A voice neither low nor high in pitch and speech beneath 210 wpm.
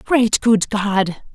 No: high, 215 Hz; slow, 135 wpm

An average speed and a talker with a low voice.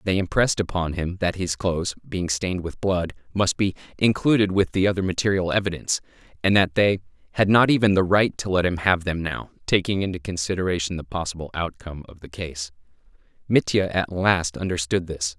Yes: average, 185 wpm; very low, 90 Hz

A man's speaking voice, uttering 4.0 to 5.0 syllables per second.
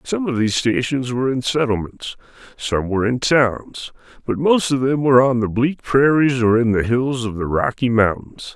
Yes: male; 4.9 syllables/s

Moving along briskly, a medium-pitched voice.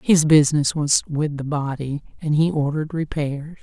No: average, 165 wpm; medium, 150 Hz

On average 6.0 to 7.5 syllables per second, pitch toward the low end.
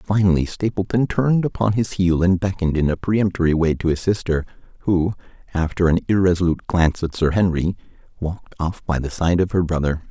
Yes: 6.1 syllables/s; very low, 90 Hz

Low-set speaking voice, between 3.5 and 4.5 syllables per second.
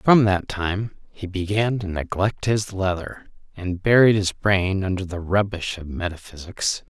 Yes: very low, 95 Hz; 4.2 syllables/s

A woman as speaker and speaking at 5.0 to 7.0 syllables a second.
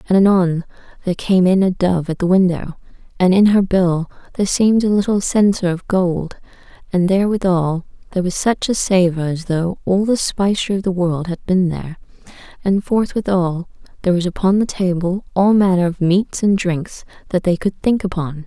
Yes: female; 5.5 syllables/s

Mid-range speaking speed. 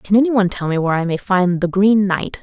No: fast, 270 wpm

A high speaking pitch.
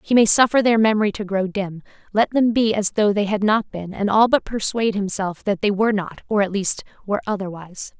Yes: high, 205 Hz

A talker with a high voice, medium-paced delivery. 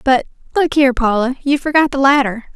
Yes: very high, 270 Hz; average, 190 wpm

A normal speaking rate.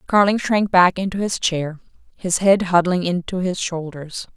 Yes: average, 165 wpm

